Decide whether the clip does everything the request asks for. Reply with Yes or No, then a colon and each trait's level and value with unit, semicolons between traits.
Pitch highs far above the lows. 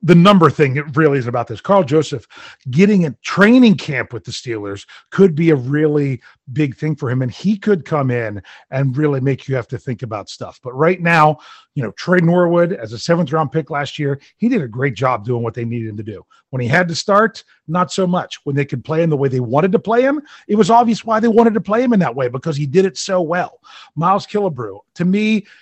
Yes: wide, 6.4 semitones